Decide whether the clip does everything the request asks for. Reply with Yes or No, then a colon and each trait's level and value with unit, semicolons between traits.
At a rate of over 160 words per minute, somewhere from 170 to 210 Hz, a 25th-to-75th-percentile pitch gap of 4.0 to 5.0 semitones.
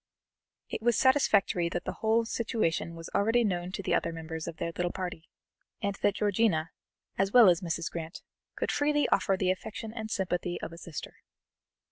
Yes: average, 180 wpm; high, 190 Hz; average, 4.6 semitones